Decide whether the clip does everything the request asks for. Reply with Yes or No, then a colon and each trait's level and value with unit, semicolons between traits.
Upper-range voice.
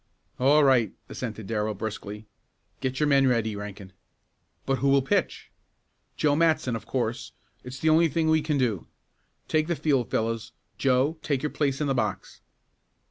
No: low, 130 Hz